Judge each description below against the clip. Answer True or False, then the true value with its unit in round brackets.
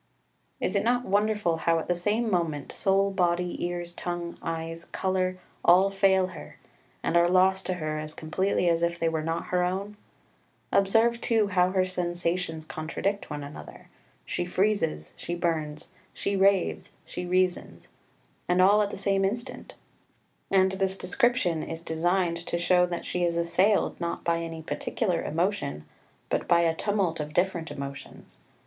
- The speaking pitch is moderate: True (180 Hz)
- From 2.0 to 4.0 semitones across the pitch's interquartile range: True (2.6 semitones)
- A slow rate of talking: False (165 wpm)